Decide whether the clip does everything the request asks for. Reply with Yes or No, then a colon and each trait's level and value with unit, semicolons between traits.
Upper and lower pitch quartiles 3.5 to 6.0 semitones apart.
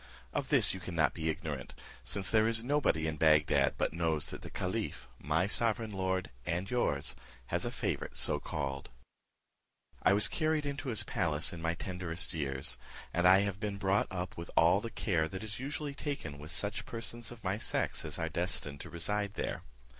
Yes: average, 5.1 semitones